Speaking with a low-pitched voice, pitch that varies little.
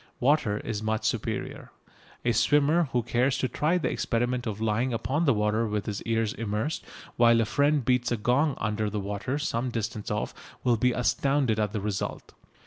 No: low, 115 Hz; average, 3.4 semitones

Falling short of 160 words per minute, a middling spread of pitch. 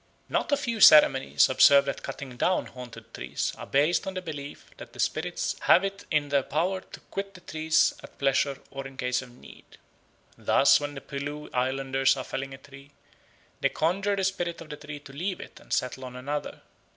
No: average, 200 wpm; average, 4.2 semitones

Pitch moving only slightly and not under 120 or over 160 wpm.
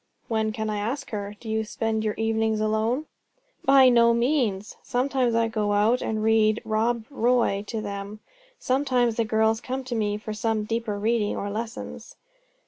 No: narrow, 1.8 semitones; average, 170 wpm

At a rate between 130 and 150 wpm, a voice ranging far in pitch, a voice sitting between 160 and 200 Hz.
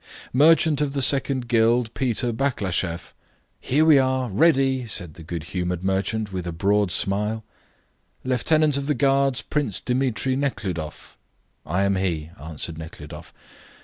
No: average, 140 wpm; wide, 7.0 semitones; low, 115 Hz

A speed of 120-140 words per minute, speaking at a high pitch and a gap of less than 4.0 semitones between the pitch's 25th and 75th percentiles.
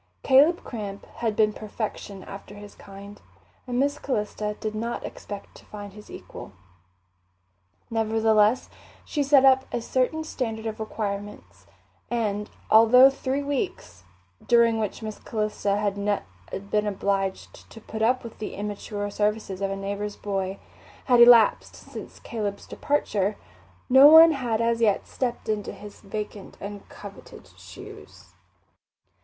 Yes: slow, 135 wpm; high, 215 Hz; average, 2.7 semitones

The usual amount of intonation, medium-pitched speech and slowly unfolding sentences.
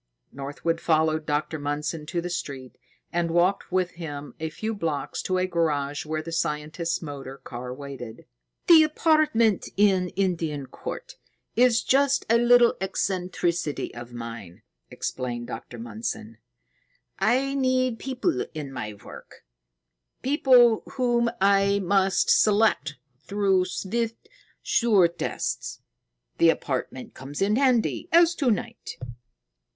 No: wide, 7.6 semitones; medium, 175 Hz; slow, 125 wpm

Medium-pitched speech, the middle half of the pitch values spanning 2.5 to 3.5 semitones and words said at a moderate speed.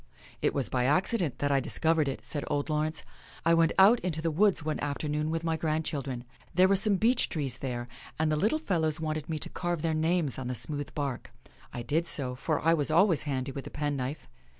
No: medium, 155 Hz; average, 2.9 semitones; fast, 225 wpm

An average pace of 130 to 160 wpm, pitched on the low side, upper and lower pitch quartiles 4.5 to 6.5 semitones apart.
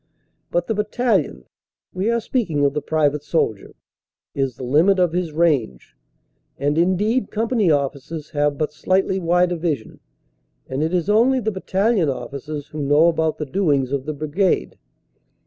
No: average, 155 wpm; medium, 160 Hz; average, 4.8 semitones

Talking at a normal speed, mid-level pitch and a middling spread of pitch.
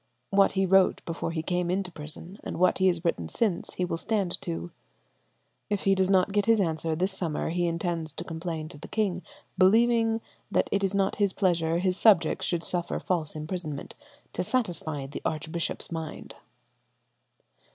Yes: average, 175 wpm; medium, 175 Hz; average, 3.0 semitones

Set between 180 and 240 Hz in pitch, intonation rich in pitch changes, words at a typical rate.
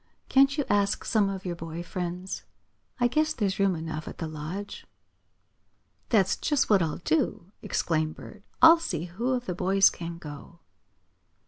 No: medium, 185 Hz; average, 4.7 semitones; average, 160 wpm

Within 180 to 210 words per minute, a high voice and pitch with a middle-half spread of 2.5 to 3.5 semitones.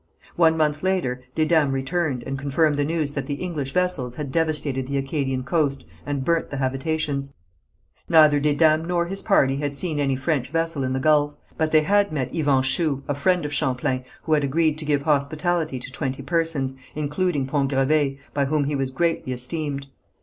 No: average, 185 wpm; medium, 145 Hz; average, 2.9 semitones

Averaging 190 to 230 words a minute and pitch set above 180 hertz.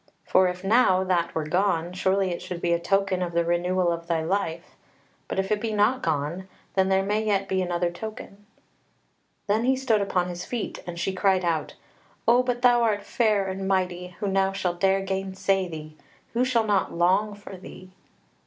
Yes: average, 195 wpm; high, 190 Hz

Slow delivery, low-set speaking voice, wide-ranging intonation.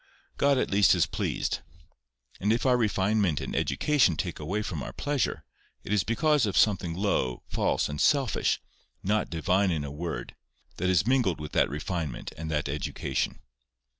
No: average, 165 wpm; very low, 95 Hz; wide, 5.8 semitones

